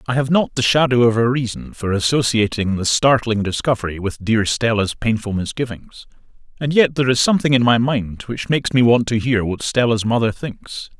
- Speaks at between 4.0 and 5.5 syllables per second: Yes, 5.4 syllables/s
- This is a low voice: Yes, low, 115 Hz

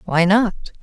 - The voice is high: Yes, high, 195 Hz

